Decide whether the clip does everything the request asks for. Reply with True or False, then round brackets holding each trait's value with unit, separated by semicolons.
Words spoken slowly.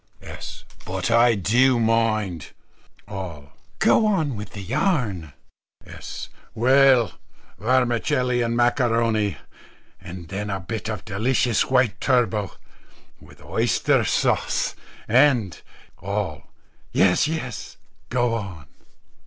True (105 wpm)